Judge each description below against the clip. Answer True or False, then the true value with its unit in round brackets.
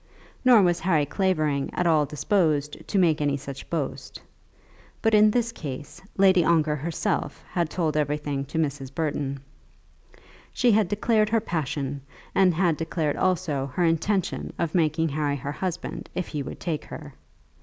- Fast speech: False (155 wpm)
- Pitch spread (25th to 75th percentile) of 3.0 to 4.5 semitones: True (4.2 semitones)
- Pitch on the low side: False (160 Hz)